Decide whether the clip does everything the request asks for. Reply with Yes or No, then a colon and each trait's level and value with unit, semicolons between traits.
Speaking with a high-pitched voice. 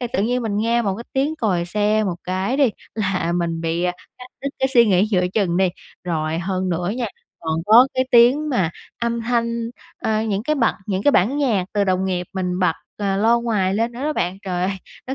Yes: high, 205 Hz